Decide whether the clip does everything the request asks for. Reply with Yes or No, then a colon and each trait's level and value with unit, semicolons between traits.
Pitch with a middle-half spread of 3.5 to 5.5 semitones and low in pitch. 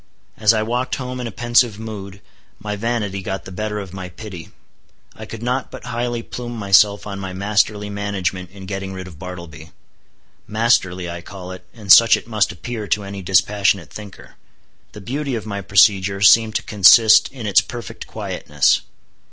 No: average, 3.0 semitones; low, 100 Hz